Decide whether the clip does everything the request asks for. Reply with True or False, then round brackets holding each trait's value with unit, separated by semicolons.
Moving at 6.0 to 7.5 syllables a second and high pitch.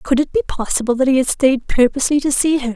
True (6.5 syllables/s; 265 Hz)